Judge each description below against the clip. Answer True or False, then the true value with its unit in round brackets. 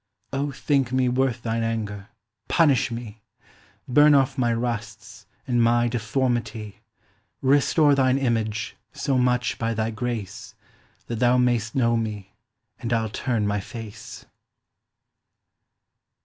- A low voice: True (120 Hz)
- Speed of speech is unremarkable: False (110 wpm)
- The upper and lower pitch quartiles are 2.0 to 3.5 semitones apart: True (2.5 semitones)